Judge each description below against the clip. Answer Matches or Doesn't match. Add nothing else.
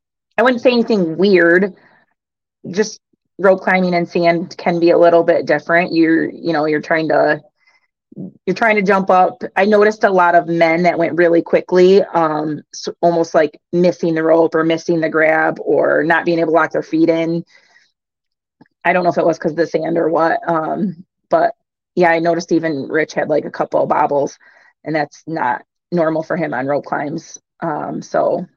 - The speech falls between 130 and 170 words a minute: Doesn't match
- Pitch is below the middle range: Doesn't match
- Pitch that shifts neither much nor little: Doesn't match